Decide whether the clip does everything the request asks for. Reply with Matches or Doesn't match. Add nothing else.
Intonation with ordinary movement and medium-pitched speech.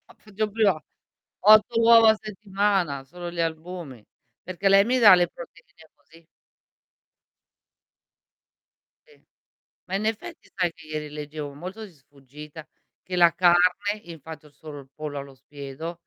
Matches